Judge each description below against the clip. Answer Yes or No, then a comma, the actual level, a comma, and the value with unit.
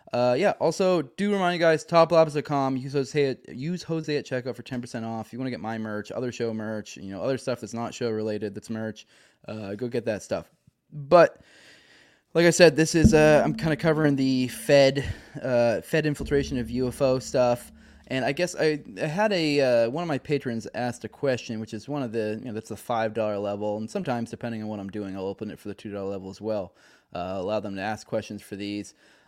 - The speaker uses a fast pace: Yes, fast, 230 wpm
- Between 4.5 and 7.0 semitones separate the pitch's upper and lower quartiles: Yes, average, 5.0 semitones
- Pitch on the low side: Yes, low, 125 Hz